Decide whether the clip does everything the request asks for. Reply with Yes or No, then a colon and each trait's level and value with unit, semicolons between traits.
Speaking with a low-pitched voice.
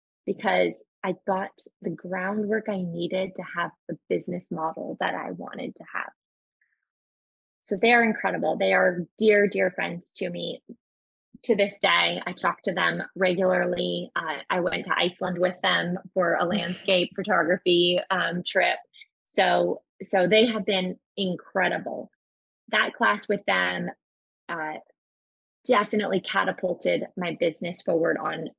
No: medium, 185 Hz